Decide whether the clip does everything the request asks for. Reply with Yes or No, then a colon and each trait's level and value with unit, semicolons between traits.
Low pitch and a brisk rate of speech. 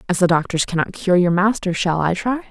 No: medium, 185 Hz; fast, 240 wpm